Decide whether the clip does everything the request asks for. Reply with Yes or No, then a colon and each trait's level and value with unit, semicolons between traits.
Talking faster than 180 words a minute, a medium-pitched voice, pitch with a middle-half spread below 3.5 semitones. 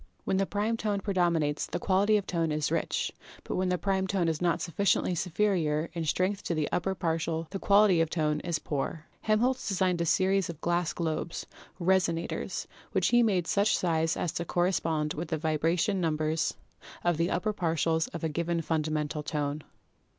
Yes: average, 190 wpm; medium, 170 Hz; average, 3.0 semitones